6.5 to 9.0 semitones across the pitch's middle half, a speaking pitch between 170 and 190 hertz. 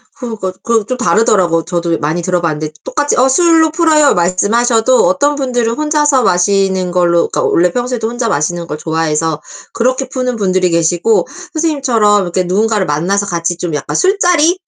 No: wide, 6.8 semitones; high, 210 Hz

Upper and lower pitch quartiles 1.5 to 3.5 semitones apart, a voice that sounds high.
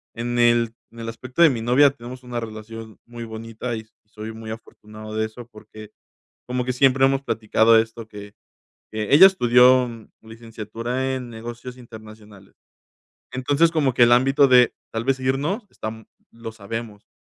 No: narrow, 2.4 semitones; low, 115 Hz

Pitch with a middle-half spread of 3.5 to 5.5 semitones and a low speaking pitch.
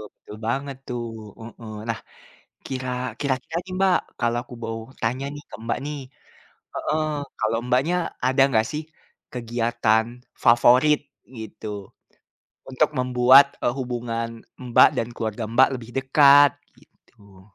No: average, 3.1 semitones; low, 125 Hz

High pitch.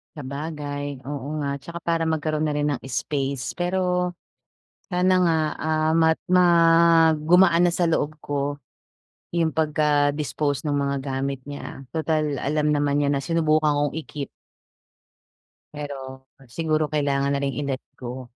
No: medium, 150 Hz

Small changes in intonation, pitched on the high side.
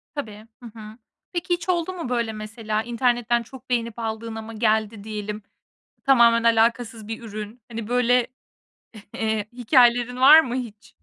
Yes: narrow, 2.2 semitones; high, 230 Hz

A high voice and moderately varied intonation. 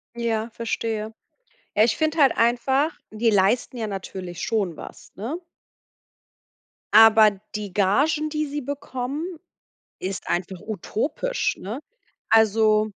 Yes: high, 225 Hz; average, 4.5 semitones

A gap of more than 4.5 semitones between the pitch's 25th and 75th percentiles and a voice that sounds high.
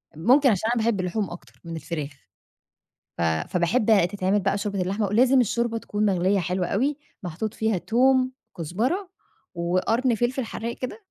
Yes: average, 5.1 semitones; high, 205 Hz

